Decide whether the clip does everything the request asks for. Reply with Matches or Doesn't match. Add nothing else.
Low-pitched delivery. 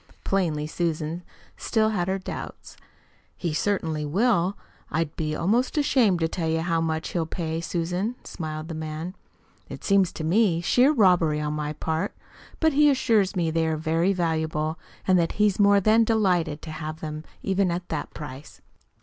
Doesn't match